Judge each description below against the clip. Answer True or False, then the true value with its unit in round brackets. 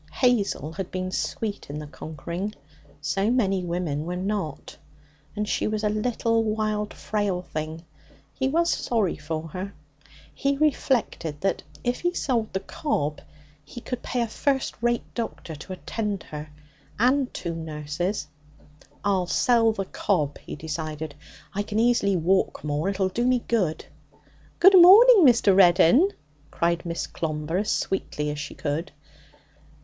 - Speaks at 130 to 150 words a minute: True (145 wpm)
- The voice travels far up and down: True (6.3 semitones)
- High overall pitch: True (195 Hz)